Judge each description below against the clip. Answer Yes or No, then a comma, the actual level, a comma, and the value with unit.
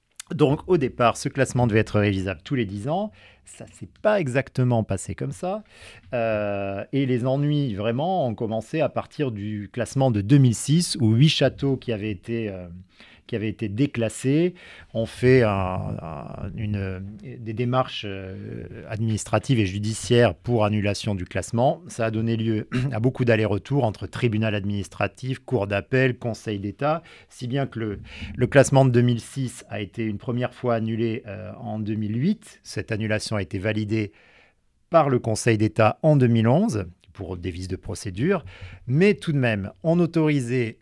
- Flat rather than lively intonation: No, average, 4.2 semitones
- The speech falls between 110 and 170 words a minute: Yes, average, 165 wpm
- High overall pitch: No, low, 115 Hz